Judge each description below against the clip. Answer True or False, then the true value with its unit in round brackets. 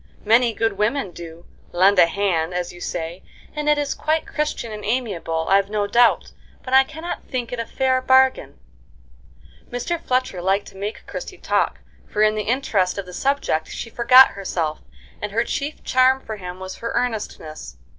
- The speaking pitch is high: True (215 Hz)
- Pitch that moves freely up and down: True (5.8 semitones)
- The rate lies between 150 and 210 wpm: True (180 wpm)